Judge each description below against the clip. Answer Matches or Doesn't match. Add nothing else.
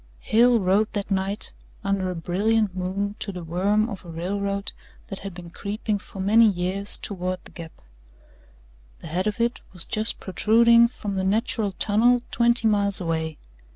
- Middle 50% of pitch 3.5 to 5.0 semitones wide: Doesn't match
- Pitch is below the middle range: Doesn't match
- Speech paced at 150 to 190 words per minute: Matches